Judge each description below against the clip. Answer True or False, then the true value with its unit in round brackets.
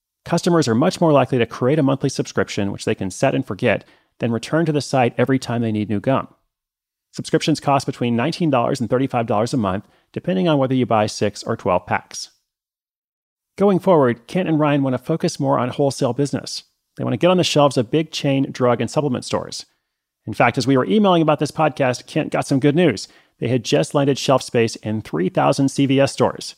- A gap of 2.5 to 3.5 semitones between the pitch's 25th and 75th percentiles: False (4.2 semitones)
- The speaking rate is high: True (210 wpm)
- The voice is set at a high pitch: False (135 Hz)